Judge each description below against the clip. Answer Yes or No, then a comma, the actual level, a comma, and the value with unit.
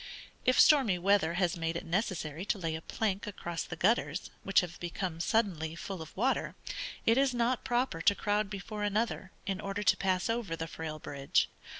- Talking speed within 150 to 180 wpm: No, average, 190 wpm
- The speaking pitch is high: Yes, high, 195 Hz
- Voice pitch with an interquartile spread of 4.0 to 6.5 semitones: Yes, average, 4.4 semitones